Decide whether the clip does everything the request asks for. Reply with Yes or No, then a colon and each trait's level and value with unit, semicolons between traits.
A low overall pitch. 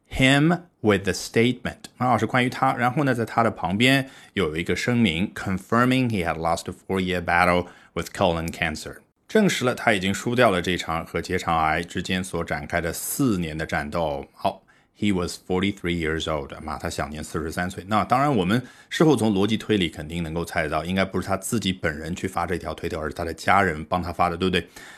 Yes: very low, 90 Hz